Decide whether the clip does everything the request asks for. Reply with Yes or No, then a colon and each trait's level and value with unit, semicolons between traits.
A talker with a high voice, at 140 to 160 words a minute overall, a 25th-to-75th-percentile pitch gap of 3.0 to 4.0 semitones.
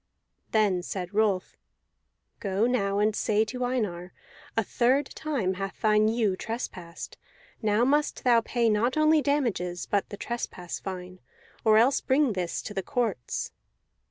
No: high, 215 Hz; average, 145 wpm; average, 4.4 semitones